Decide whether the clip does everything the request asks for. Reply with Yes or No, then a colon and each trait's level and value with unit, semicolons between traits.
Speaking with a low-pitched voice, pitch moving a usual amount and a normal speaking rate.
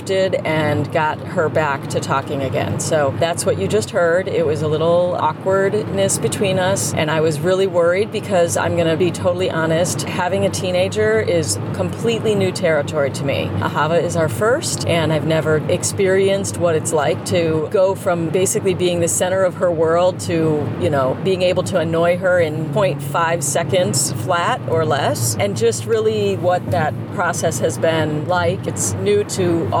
No: medium, 165 Hz; average, 3.8 semitones; average, 175 wpm